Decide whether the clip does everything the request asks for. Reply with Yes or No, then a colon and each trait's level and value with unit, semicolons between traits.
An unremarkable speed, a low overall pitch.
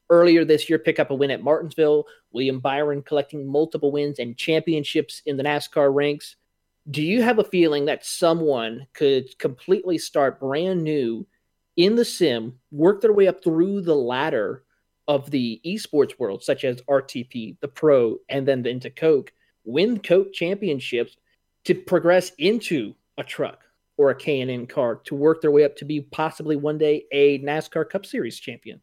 No: average, 175 wpm; medium, 150 Hz